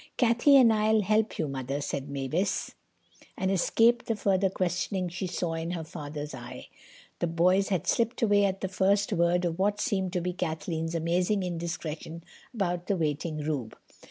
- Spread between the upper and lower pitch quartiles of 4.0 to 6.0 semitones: No, average, 3.6 semitones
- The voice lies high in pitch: No, medium, 180 Hz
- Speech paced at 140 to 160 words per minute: No, average, 170 wpm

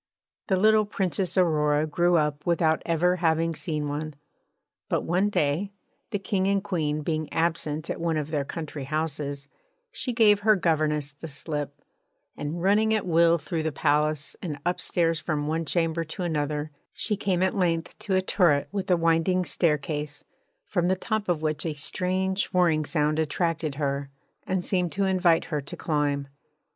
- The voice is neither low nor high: Yes, medium, 165 Hz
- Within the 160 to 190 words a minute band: Yes, average, 170 wpm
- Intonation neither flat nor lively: Yes, average, 3.4 semitones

